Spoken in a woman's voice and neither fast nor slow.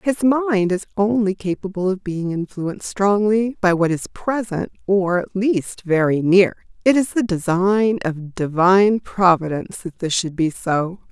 Yes: female; average, 160 wpm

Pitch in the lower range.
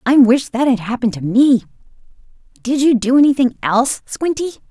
No: very high, 250 Hz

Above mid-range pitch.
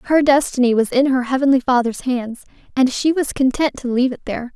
Yes: very high, 260 Hz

